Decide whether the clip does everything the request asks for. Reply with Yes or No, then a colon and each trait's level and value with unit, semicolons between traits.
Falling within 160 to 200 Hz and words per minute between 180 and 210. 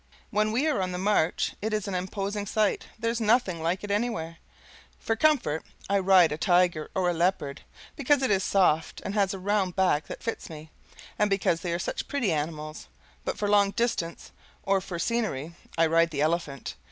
Yes: high, 190 Hz; average, 195 wpm